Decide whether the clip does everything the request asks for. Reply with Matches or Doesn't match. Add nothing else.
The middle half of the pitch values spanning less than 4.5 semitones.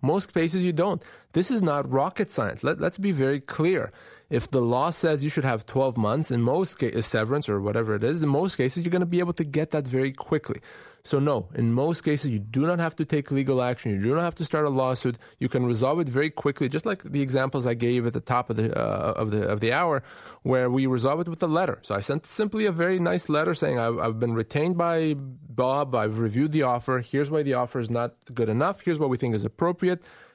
Doesn't match